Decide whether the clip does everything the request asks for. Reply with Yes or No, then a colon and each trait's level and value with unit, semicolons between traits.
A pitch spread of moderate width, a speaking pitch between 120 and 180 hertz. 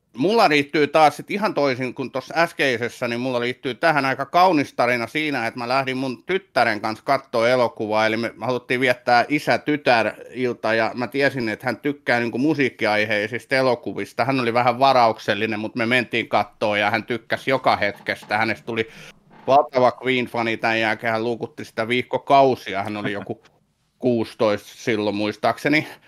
Yes: average, 3.4 semitones; low, 125 Hz